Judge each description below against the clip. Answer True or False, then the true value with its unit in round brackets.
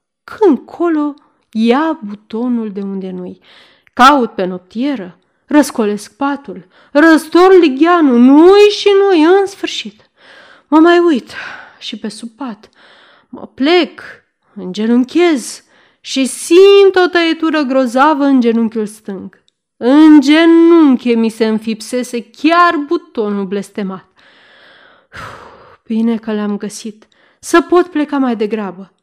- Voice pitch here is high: True (265 Hz)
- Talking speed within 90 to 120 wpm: True (115 wpm)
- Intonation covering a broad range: True (7.2 semitones)